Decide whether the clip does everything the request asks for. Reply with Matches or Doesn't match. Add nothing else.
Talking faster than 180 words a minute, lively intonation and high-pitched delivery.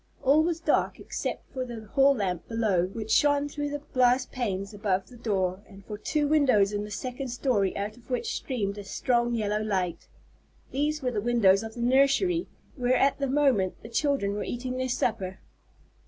Doesn't match